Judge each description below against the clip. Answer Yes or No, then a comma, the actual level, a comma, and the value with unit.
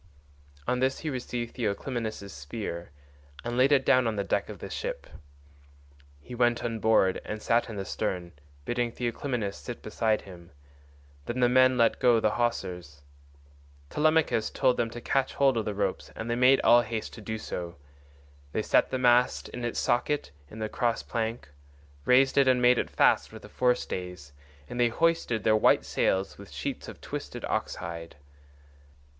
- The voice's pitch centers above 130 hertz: No, low, 120 Hz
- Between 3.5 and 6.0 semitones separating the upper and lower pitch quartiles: No, average, 3.1 semitones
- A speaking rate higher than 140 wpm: Yes, average, 175 wpm